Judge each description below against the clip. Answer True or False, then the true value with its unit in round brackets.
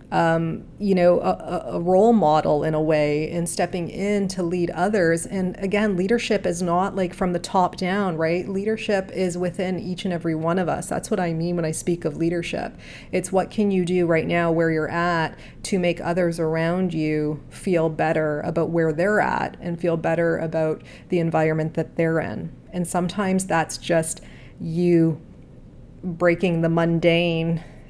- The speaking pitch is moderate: True (170 Hz)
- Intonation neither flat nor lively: False (2.1 semitones)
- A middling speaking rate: True (180 wpm)